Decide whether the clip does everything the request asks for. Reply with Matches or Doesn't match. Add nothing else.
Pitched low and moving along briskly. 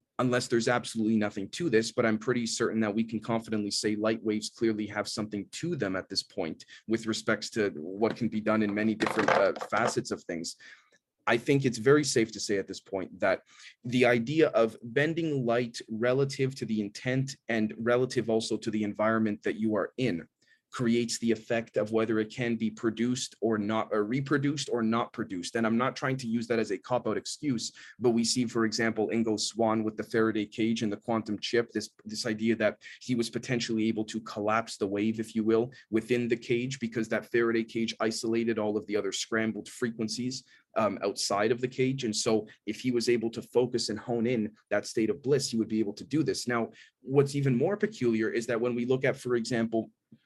Matches